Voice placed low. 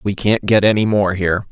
Yes: low, 100 Hz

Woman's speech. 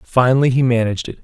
No: male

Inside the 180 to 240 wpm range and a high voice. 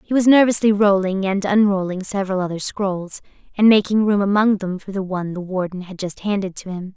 Yes: fast, 205 wpm; high, 195 Hz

